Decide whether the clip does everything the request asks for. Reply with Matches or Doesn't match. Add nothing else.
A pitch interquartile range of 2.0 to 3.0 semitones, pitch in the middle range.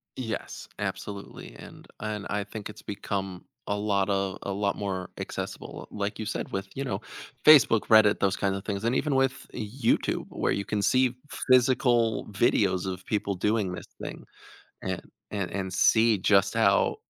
Doesn't match